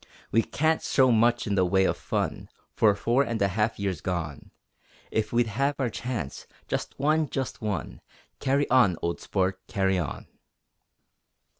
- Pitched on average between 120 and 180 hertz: No, low, 110 Hz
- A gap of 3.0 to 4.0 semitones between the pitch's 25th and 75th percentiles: No, average, 5.2 semitones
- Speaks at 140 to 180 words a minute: Yes, average, 160 wpm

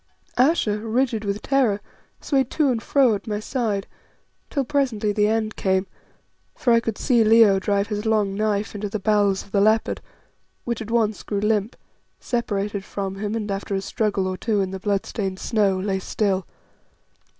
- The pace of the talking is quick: No, average, 175 wpm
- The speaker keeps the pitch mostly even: Yes, narrow, 2.2 semitones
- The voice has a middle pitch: No, high, 210 Hz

